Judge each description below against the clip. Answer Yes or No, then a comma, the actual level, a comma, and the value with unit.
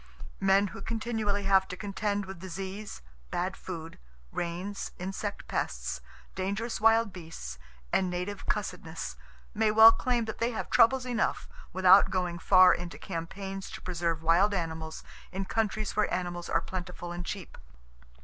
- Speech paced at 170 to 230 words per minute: No, average, 145 wpm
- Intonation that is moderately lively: Yes, average, 3.0 semitones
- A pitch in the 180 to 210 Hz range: Yes, high, 190 Hz